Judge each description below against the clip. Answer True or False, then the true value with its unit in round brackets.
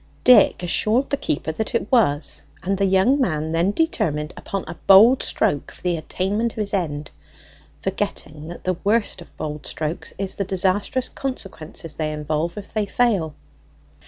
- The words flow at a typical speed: True (165 wpm)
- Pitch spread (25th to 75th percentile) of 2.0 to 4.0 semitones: False (5.4 semitones)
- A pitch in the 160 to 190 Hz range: True (185 Hz)